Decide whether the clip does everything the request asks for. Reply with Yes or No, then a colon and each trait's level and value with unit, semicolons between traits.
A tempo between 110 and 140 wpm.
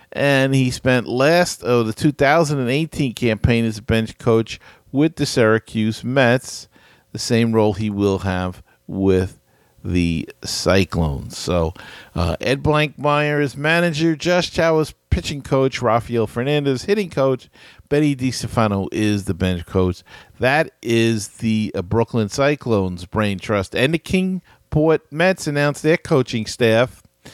Yes: slow, 135 wpm